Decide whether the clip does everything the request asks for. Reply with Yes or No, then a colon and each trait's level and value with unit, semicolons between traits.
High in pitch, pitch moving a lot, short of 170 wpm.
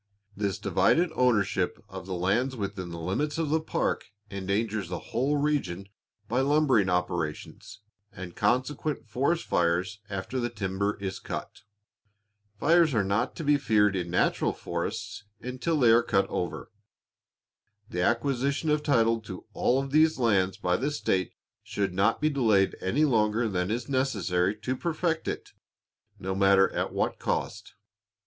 No: low, 110 Hz; wide, 6.3 semitones; average, 150 wpm